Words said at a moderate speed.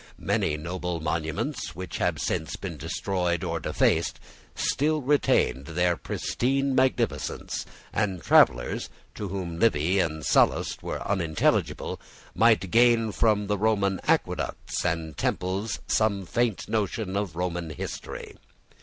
No: slow, 120 wpm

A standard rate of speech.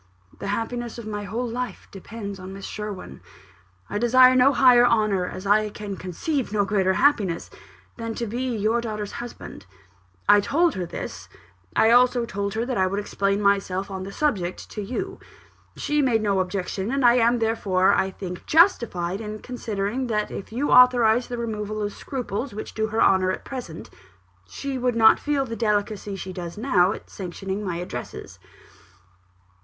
Yes: average, 175 wpm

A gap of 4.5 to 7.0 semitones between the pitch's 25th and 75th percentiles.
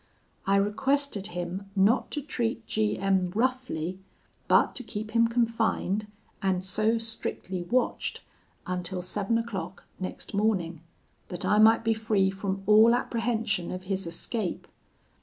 No: average, 3.3 semitones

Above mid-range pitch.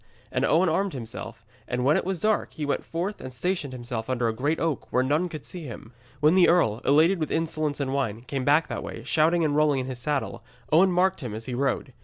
No: medium, 145 Hz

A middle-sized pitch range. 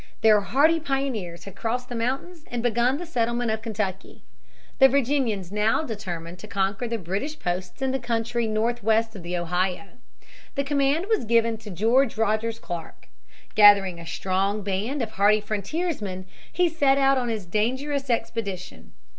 Yes: average, 4.9 semitones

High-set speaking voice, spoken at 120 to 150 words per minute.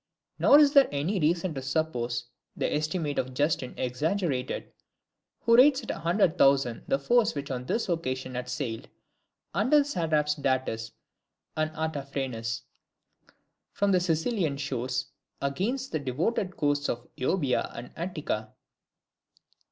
No: medium, 150 Hz; slow, 135 wpm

